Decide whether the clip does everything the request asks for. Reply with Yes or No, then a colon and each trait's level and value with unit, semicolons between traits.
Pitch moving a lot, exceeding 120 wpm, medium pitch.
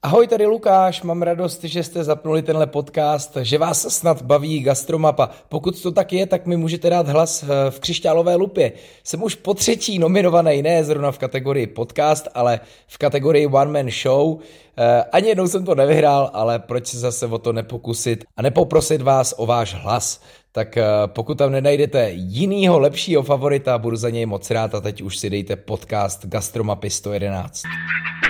Yes: wide, 6.0 semitones; fast, 170 wpm; medium, 145 Hz